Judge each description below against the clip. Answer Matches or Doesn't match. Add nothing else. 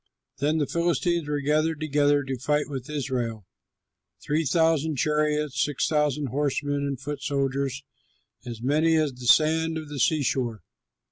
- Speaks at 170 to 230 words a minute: Doesn't match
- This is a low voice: Doesn't match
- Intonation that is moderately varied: Doesn't match